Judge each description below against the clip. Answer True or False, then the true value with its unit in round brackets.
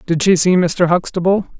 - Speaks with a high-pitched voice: False (180 Hz)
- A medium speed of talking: True (190 wpm)